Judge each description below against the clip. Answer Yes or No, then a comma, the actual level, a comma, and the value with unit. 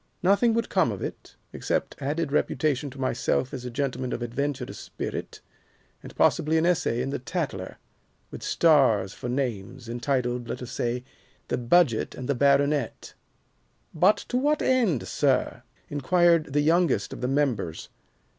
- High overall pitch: No, medium, 140 Hz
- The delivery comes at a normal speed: Yes, average, 155 wpm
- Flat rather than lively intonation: No, average, 4.6 semitones